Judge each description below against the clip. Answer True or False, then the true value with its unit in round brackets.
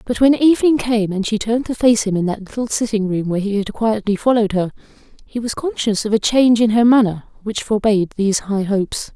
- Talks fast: True (230 wpm)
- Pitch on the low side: False (220 Hz)